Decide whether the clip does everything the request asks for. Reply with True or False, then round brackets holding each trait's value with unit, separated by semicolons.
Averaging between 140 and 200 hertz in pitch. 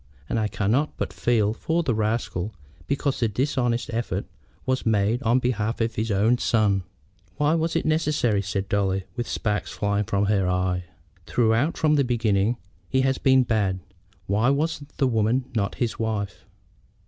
False (115 Hz)